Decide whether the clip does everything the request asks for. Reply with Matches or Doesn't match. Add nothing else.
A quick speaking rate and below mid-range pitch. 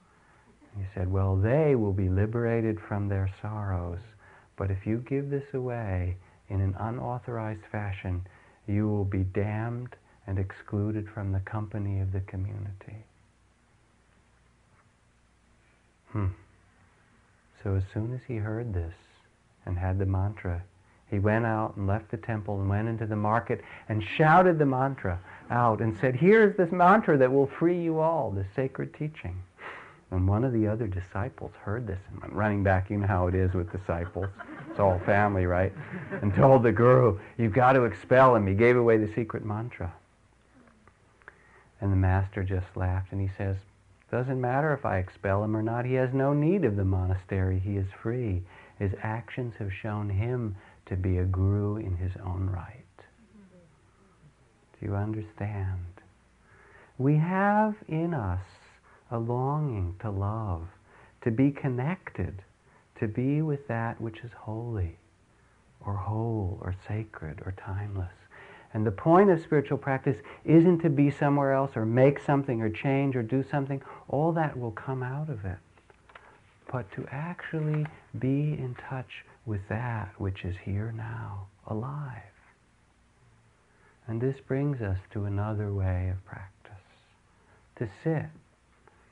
Doesn't match